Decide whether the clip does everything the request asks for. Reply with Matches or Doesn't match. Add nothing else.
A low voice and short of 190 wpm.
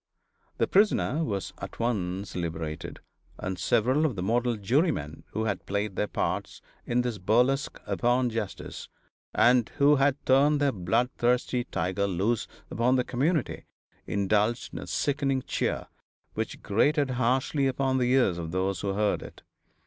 Matches